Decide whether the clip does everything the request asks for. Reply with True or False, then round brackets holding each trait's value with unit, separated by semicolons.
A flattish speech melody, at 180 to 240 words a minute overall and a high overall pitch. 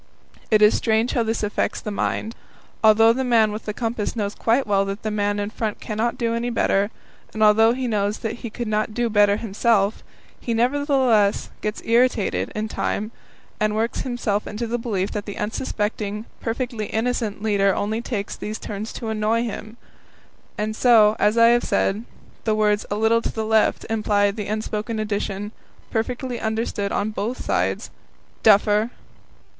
False (1.8 semitones; 170 wpm; 220 Hz)